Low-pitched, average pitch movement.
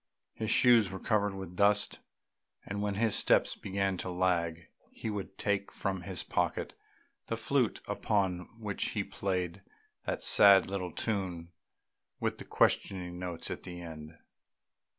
No: very low, 95 Hz; narrow, 2.3 semitones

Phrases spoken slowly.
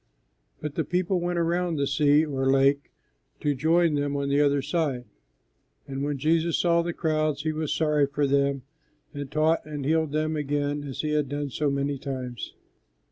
No: average, 185 wpm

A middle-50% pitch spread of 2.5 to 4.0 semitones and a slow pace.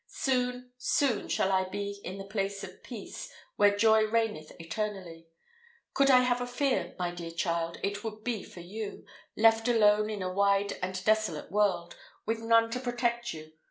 No: average, 3.5 semitones; average, 175 wpm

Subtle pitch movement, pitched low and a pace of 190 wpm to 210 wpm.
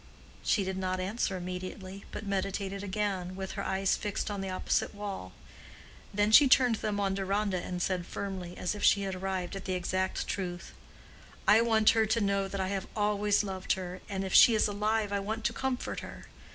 No: narrow, 1.8 semitones; high, 195 Hz; average, 200 wpm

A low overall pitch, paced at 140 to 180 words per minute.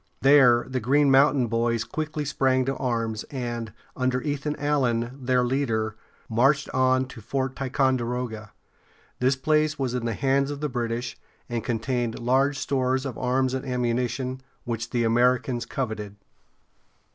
Yes: low, 125 Hz; average, 145 wpm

